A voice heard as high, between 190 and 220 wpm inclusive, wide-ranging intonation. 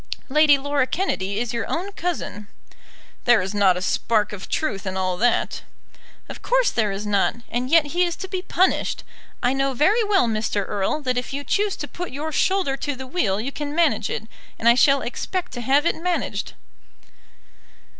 Yes: very high, 270 Hz; average, 195 wpm; wide, 7.6 semitones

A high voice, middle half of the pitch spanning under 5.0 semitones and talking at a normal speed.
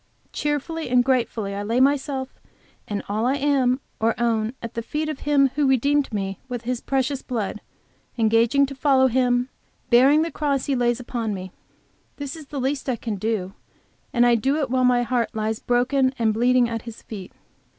Yes: very high, 250 Hz; average, 3.2 semitones; average, 190 wpm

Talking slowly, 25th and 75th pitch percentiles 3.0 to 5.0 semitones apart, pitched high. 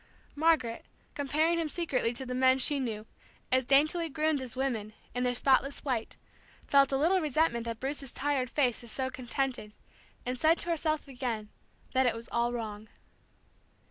No: average, 170 wpm; average, 3.5 semitones; very high, 260 Hz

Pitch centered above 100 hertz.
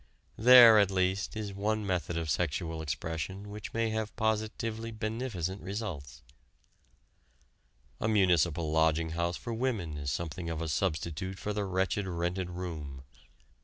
No: very low, 95 Hz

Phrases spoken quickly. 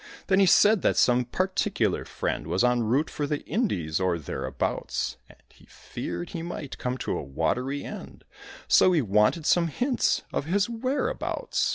No: average, 175 wpm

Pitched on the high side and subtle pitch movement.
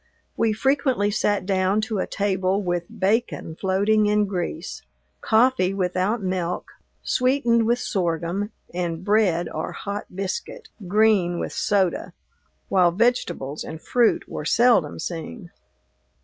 No: high, 195 Hz; average, 3.7 semitones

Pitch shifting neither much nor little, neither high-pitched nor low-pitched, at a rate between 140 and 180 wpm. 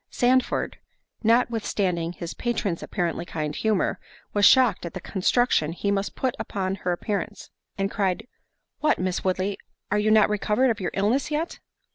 No: average, 3.9 semitones; high, 200 Hz; average, 155 wpm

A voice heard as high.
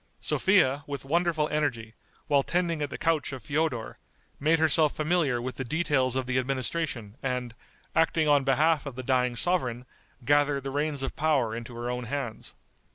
No: medium, 140 Hz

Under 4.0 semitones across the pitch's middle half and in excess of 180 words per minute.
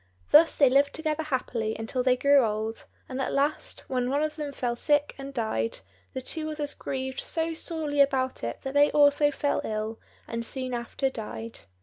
Yes: average, 3.5 semitones; average, 190 wpm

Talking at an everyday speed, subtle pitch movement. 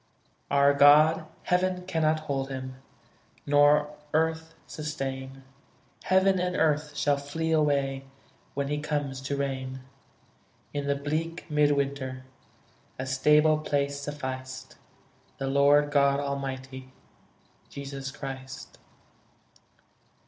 No: slow, 105 wpm; narrow, 2.0 semitones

